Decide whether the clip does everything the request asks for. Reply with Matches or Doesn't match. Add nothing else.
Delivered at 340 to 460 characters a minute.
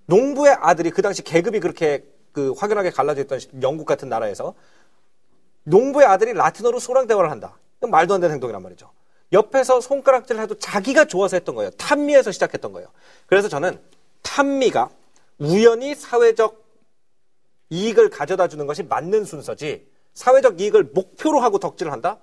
Matches